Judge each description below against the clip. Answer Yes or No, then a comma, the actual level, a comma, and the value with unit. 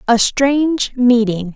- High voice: Yes, high, 245 Hz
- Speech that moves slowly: Yes, slow, 115 wpm